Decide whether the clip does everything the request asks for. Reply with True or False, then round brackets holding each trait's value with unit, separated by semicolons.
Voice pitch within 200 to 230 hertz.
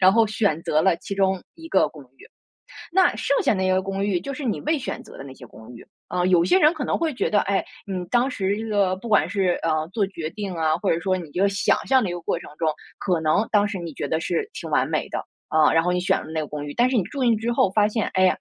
False (190 Hz)